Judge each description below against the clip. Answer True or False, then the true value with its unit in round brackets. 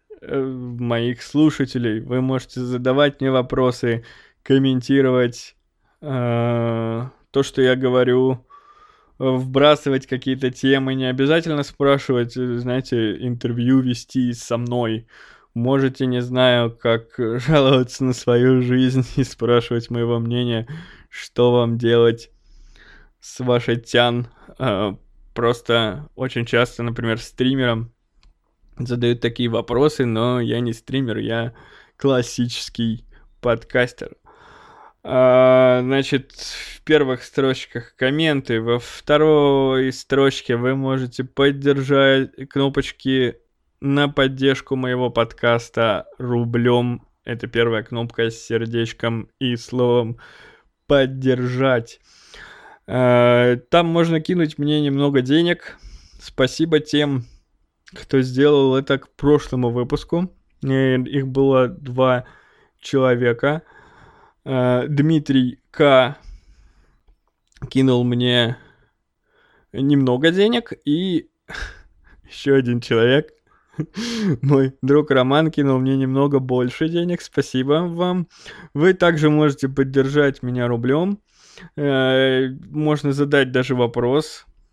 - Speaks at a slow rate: True (95 wpm)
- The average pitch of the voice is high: False (130 Hz)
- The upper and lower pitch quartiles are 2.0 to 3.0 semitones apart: True (2.5 semitones)